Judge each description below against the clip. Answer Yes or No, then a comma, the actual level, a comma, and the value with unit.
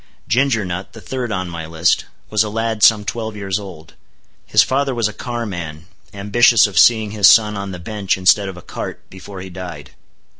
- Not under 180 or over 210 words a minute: Yes, average, 195 wpm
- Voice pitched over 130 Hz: No, low, 100 Hz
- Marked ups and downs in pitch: No, average, 3.4 semitones